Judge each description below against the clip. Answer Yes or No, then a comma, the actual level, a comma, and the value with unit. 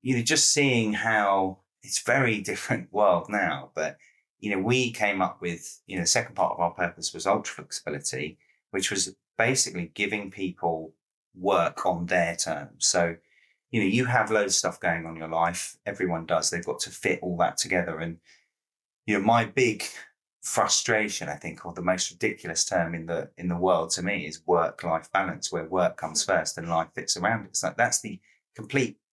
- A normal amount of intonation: Yes, average, 3.2 semitones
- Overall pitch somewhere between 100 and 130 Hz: No, very low, 90 Hz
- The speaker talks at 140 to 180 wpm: No, average, 195 wpm